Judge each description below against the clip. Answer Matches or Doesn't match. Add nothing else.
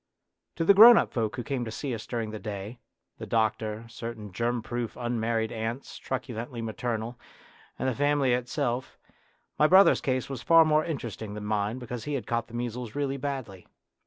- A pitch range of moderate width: Matches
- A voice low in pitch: Matches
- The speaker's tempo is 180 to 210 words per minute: Matches